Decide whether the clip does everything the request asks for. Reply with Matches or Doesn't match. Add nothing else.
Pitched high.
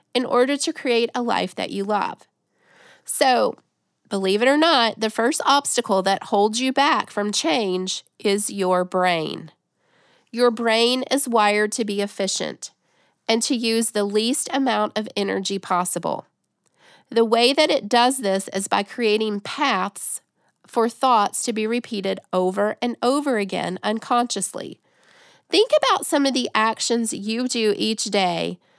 Matches